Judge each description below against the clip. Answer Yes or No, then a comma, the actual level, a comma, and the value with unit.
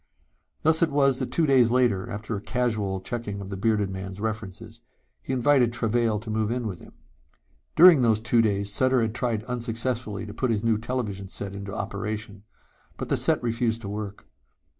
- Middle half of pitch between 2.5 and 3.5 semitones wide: Yes, average, 3.2 semitones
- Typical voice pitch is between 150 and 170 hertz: No, low, 110 Hz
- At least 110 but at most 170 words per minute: No, average, 185 wpm